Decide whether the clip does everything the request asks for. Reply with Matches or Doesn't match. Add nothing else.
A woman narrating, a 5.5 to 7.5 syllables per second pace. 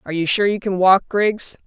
Doesn't match